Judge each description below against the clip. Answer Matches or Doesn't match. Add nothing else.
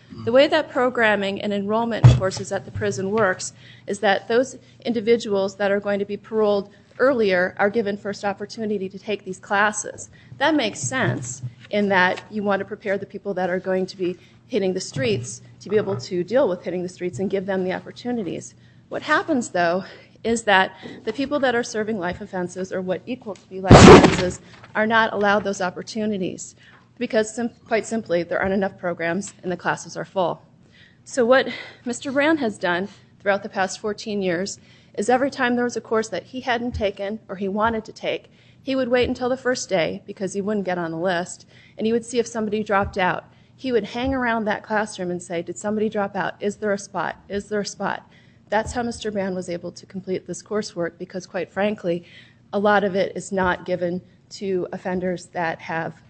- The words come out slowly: Doesn't match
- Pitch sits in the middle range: Doesn't match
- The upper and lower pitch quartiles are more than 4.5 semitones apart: Doesn't match